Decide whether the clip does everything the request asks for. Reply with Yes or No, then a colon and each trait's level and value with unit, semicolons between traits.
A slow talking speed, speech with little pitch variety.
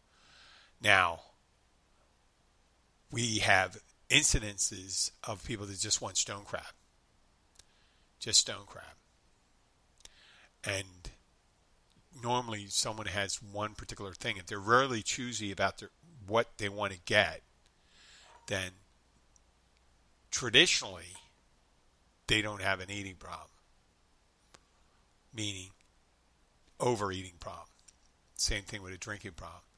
No: slow, 100 wpm; average, 4.1 semitones